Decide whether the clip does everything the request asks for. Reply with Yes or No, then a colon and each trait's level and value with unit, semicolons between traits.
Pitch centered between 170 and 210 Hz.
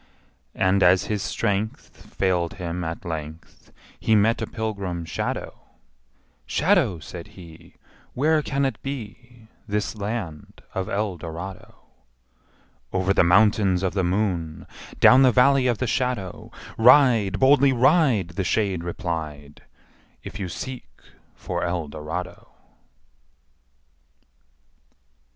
No: low, 100 Hz